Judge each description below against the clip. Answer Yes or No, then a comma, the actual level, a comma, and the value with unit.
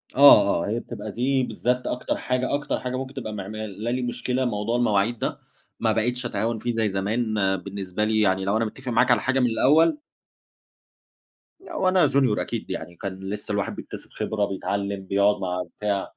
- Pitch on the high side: No, low, 110 Hz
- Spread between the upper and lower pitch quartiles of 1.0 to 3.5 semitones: No, average, 4.0 semitones